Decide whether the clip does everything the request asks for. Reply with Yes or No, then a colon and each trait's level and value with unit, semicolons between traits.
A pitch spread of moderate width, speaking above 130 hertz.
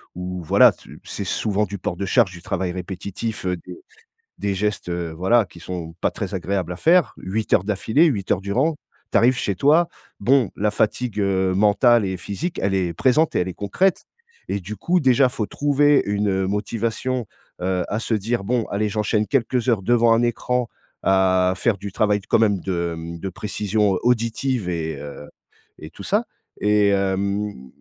No: average, 4.0 semitones; low, 100 Hz